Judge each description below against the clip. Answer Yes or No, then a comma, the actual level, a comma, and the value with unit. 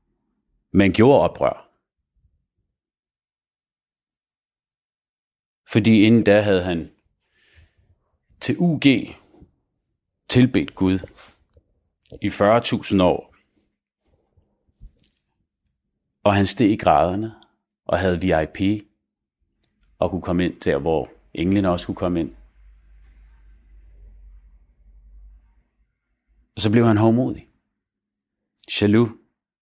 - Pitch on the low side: Yes, very low, 90 Hz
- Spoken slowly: Yes, slow, 80 wpm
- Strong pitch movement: Yes, wide, 6.0 semitones